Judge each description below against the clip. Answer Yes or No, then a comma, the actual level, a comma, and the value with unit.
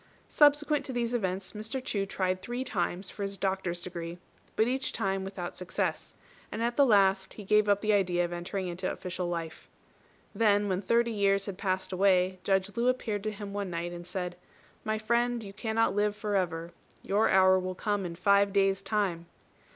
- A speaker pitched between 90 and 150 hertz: No, high, 195 Hz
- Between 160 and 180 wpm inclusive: No, average, 190 wpm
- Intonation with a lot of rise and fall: No, average, 2.7 semitones